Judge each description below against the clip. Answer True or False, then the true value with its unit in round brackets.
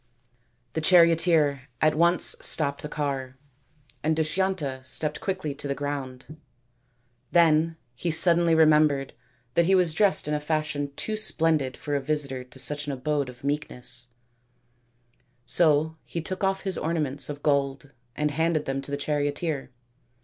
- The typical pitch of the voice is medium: True (150 Hz)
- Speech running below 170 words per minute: True (150 wpm)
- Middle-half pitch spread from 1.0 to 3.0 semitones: True (2.7 semitones)